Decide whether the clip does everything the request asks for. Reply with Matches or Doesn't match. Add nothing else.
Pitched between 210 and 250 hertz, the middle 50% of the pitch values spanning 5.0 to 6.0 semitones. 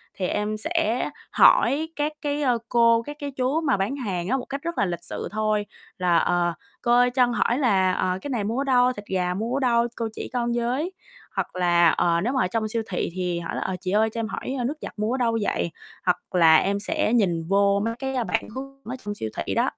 Matches